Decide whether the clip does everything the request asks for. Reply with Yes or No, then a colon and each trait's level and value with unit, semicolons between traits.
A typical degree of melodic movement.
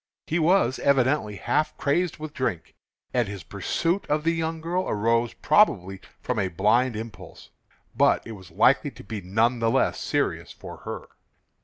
No: wide, 6.8 semitones